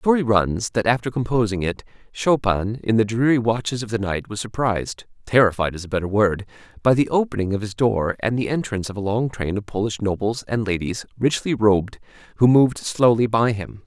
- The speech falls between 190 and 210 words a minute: Yes, average, 195 wpm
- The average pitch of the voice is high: No, low, 110 Hz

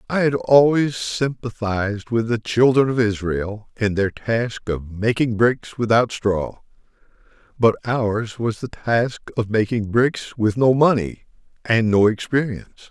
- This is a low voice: Yes, low, 115 Hz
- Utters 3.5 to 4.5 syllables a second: Yes, 4.0 syllables/s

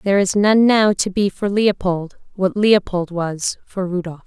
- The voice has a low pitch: No, high, 190 Hz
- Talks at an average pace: Yes, average, 185 wpm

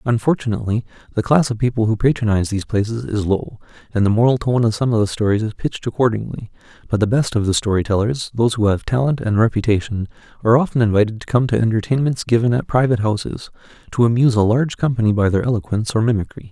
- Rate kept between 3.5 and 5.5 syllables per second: No, 7.0 syllables/s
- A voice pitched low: Yes, low, 115 Hz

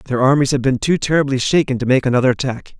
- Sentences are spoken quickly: Yes, fast, 235 wpm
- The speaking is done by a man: Yes, male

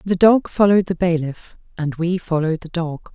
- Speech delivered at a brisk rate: No, average, 190 wpm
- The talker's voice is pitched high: No, medium, 175 Hz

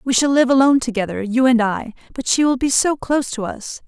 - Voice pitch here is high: Yes, very high, 250 Hz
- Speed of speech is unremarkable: No, fast, 250 wpm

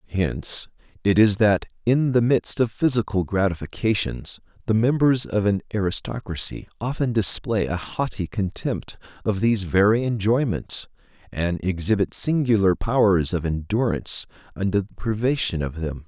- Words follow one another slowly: Yes, slow, 130 wpm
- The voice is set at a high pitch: No, low, 105 Hz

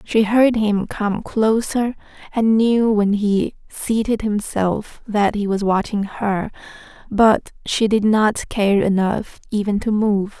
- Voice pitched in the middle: No, high, 210 Hz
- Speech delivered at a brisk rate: No, average, 145 wpm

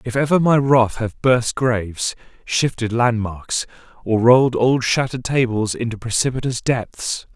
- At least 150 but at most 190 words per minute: No, average, 140 wpm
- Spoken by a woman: No, male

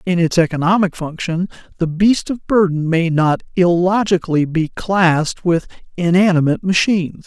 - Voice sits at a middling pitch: Yes, medium, 175 Hz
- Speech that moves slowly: Yes, slow, 130 wpm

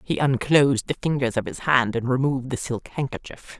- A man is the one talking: No, female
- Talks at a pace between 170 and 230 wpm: Yes, average, 200 wpm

